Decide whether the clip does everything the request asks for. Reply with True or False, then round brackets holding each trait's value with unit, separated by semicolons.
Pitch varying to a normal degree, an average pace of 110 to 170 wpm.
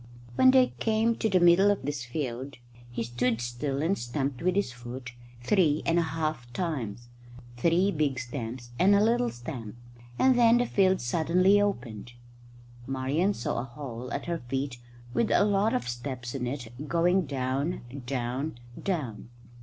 False (7.2 semitones; 160 wpm)